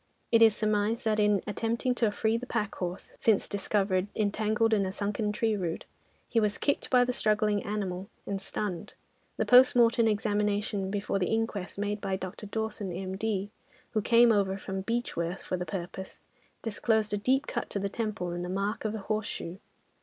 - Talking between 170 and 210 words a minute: Yes, average, 185 wpm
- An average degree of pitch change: No, narrow, 2.3 semitones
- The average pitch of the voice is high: Yes, high, 210 Hz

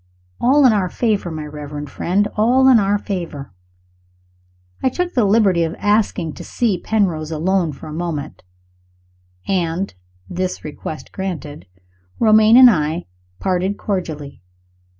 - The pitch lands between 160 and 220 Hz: Yes, medium, 185 Hz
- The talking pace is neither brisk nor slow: No, slow, 130 wpm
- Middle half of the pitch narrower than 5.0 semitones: No, wide, 5.4 semitones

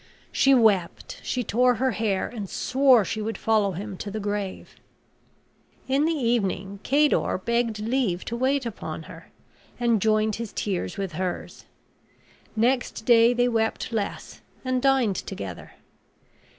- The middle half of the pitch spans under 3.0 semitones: No, average, 3.6 semitones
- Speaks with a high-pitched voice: Yes, high, 225 Hz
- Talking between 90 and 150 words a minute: Yes, average, 140 wpm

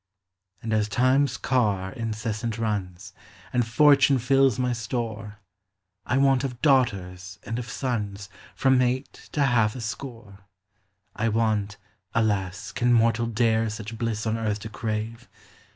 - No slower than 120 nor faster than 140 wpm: Yes, slow, 135 wpm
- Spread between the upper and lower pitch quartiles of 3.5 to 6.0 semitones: No, average, 2.8 semitones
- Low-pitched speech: Yes, low, 115 Hz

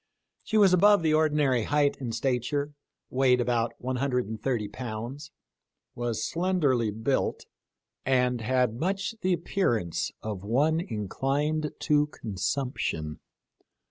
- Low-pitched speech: Yes, low, 130 Hz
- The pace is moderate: No, slow, 110 wpm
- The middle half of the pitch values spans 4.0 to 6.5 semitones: Yes, average, 4.6 semitones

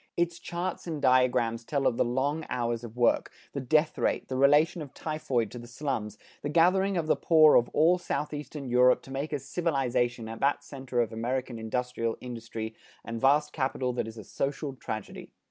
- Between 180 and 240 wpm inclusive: Yes, average, 190 wpm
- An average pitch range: Yes, average, 4.1 semitones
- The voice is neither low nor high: No, low, 130 Hz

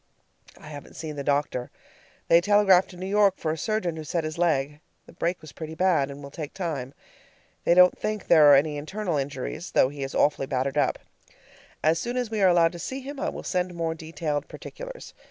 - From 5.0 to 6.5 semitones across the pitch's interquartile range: No, average, 4.2 semitones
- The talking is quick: Yes, fast, 215 wpm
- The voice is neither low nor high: Yes, medium, 165 Hz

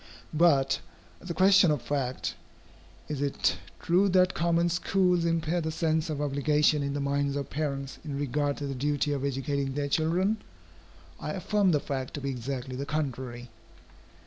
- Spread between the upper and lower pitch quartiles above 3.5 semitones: No, average, 3.2 semitones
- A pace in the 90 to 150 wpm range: No, average, 170 wpm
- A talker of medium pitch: Yes, medium, 145 Hz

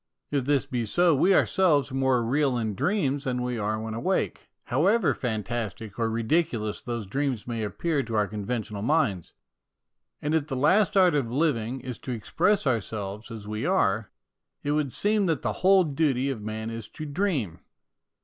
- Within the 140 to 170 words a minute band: No, average, 180 wpm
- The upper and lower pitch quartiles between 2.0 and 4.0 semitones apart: No, wide, 5.5 semitones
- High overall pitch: No, low, 130 Hz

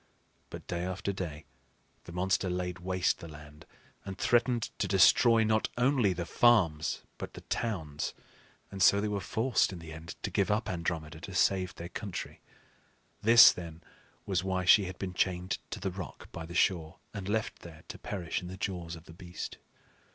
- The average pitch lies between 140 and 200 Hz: No, very low, 90 Hz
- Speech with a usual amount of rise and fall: Yes, average, 3.0 semitones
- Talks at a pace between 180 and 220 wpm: Yes, average, 185 wpm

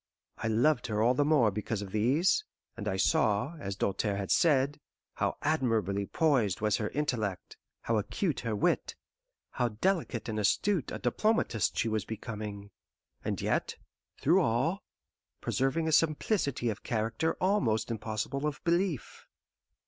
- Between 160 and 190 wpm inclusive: No, average, 145 wpm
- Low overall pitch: Yes, low, 120 Hz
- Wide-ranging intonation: Yes, wide, 6.3 semitones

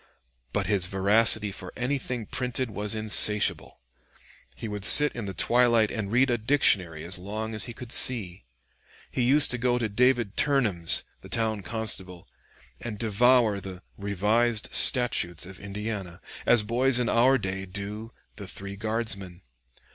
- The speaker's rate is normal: Yes, average, 150 wpm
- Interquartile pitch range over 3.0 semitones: Yes, average, 3.5 semitones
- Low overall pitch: Yes, low, 110 Hz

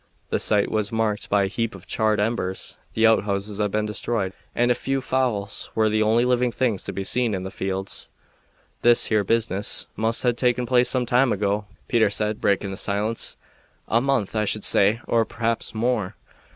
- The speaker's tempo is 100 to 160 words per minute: No, average, 190 wpm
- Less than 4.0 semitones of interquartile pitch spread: Yes, average, 2.8 semitones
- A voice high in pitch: No, low, 110 Hz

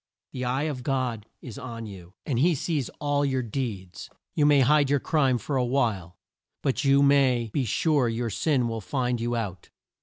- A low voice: Yes, low, 130 Hz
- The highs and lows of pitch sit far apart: No, average, 3.5 semitones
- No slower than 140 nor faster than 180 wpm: No, average, 190 wpm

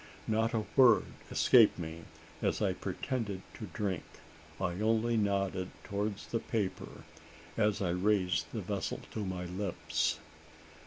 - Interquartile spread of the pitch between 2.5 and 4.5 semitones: Yes, average, 3.0 semitones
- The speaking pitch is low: Yes, low, 100 Hz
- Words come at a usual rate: No, slow, 130 wpm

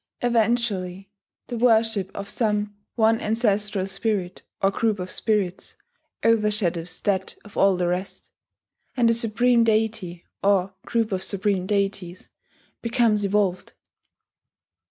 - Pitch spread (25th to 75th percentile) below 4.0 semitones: Yes, average, 2.9 semitones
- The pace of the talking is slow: Yes, slow, 115 wpm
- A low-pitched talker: No, high, 205 Hz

